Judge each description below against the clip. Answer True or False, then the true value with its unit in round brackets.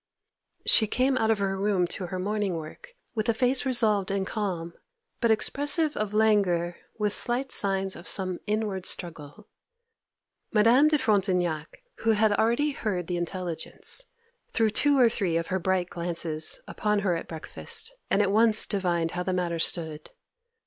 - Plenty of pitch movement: False (3.9 semitones)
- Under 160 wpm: False (165 wpm)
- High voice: True (200 Hz)